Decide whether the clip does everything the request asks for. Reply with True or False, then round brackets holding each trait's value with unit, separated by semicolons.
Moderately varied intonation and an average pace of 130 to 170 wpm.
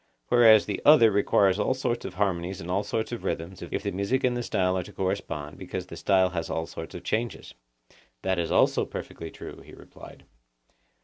False (3.6 semitones; 200 wpm)